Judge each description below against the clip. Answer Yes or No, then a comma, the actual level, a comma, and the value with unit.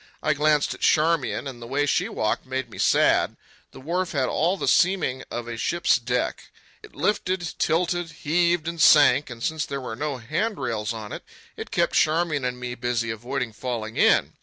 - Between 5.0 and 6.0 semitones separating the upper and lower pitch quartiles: Yes, wide, 5.4 semitones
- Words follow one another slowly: No, average, 185 wpm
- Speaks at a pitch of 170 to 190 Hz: No, medium, 140 Hz